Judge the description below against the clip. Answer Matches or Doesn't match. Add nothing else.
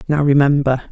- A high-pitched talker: Doesn't match